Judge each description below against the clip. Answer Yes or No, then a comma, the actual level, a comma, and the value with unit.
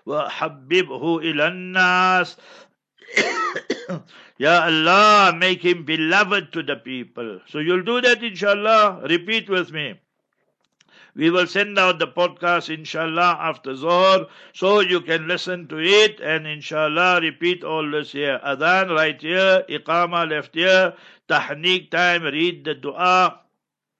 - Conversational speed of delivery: No, slow, 130 wpm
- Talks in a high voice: No, medium, 175 Hz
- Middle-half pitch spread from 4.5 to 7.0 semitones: No, narrow, 2.6 semitones